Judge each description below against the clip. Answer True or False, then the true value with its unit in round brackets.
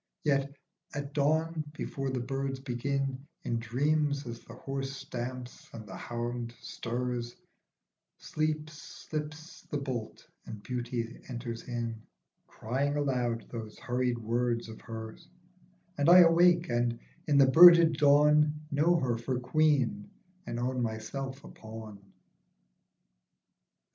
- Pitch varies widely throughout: False (3.7 semitones)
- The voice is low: True (130 Hz)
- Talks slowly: True (125 wpm)